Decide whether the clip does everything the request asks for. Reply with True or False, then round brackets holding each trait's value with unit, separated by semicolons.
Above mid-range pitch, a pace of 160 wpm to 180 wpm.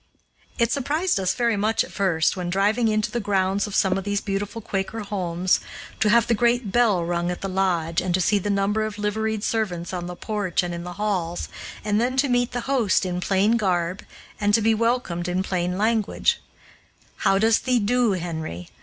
False (200 Hz; 205 wpm)